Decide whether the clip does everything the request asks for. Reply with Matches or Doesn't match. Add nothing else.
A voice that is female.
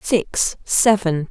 Matches